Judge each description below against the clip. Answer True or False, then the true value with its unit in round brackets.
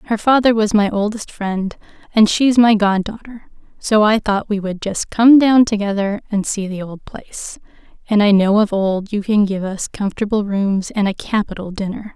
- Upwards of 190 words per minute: True (200 wpm)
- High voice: True (210 Hz)